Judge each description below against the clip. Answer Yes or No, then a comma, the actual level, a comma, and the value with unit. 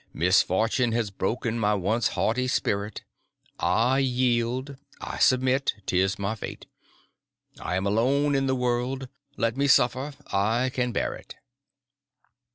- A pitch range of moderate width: Yes, average, 3.5 semitones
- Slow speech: Yes, slow, 120 wpm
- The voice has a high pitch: No, low, 120 Hz